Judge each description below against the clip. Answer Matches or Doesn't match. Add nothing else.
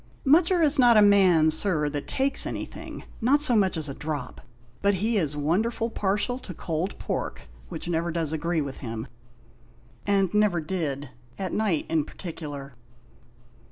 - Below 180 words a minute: Matches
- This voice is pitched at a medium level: Matches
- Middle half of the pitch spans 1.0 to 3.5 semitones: Doesn't match